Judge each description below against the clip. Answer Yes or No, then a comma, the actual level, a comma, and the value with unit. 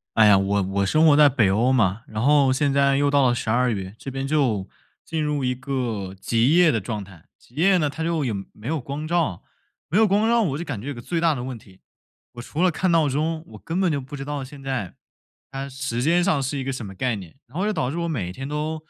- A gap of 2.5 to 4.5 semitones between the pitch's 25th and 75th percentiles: No, average, 4.9 semitones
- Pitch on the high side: No, low, 135 Hz